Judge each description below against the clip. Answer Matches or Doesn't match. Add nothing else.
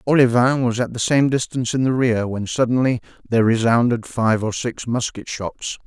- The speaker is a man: Matches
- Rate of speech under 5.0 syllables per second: Doesn't match